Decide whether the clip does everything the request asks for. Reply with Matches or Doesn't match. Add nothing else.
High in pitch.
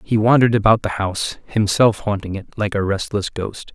Doesn't match